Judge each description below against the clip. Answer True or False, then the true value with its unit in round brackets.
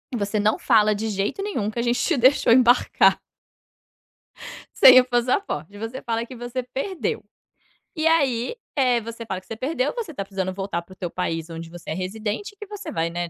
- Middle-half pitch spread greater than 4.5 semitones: True (4.9 semitones)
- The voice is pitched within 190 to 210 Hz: False (230 Hz)